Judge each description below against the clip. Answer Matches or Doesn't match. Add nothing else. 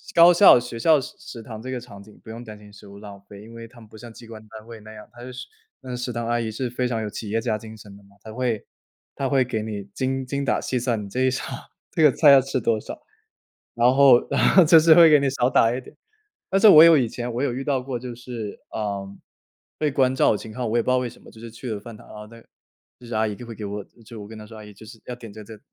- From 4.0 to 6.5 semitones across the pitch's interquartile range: Doesn't match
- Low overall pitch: Matches